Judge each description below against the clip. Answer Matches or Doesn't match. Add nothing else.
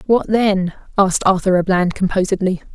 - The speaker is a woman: Matches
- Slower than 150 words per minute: Doesn't match